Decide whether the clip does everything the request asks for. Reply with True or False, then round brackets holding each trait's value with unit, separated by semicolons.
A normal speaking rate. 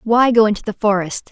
False (230 wpm)